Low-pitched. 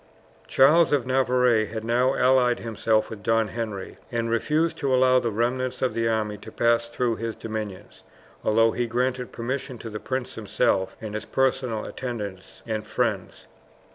Yes: low, 115 Hz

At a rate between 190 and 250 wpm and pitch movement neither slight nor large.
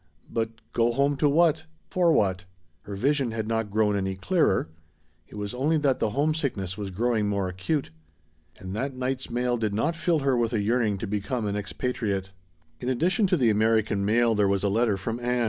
Yes: average, 200 wpm; average, 4.9 semitones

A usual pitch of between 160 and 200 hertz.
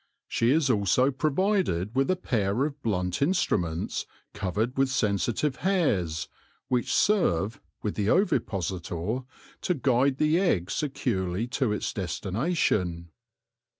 No: low, 115 Hz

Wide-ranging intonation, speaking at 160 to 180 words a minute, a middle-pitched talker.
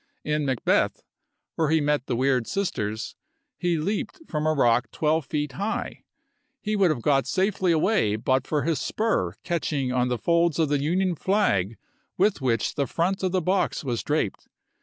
Yes: wide, 5.7 semitones; average, 175 wpm; medium, 150 Hz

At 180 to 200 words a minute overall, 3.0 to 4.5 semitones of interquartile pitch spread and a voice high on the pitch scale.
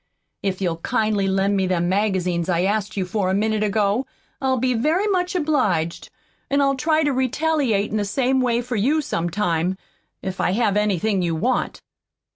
No: average, 185 wpm; wide, 5.5 semitones; high, 210 Hz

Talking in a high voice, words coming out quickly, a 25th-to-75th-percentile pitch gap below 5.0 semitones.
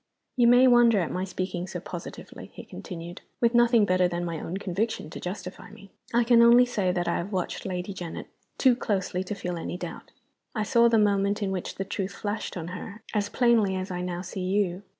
Yes: high, 195 Hz; fast, 215 wpm; average, 3.9 semitones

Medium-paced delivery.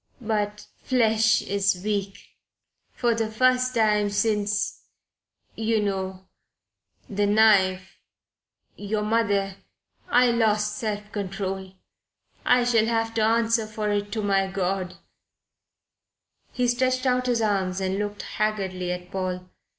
No: slow, 120 wpm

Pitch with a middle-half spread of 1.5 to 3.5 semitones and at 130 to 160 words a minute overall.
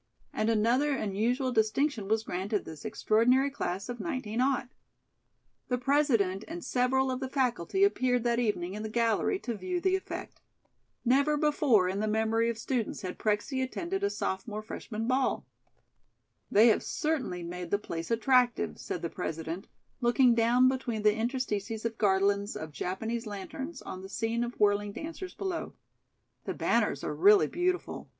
No: average, 4.3 semitones; average, 155 wpm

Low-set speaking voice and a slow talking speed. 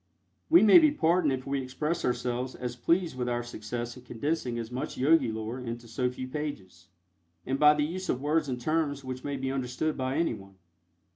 No: low, 130 Hz; average, 200 wpm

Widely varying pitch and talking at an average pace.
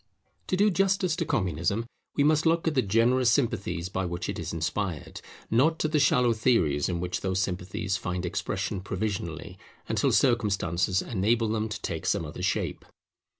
Yes: wide, 6.1 semitones; average, 170 wpm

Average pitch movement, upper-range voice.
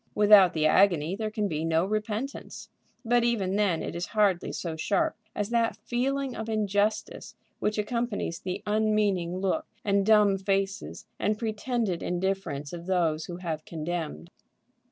Yes: average, 3.6 semitones; high, 200 Hz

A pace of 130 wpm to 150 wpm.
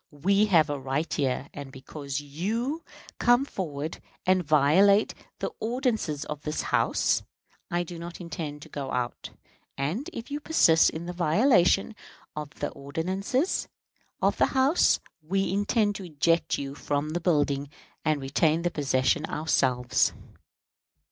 Yes: average, 140 wpm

